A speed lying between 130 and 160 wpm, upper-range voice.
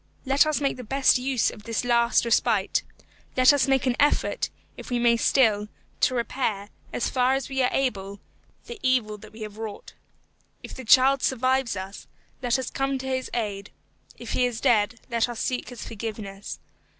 No: average, 185 wpm; high, 245 Hz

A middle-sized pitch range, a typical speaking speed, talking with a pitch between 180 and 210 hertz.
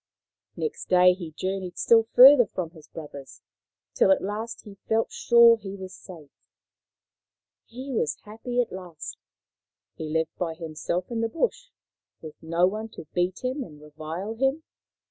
No: wide, 5.8 semitones; average, 155 wpm; high, 190 Hz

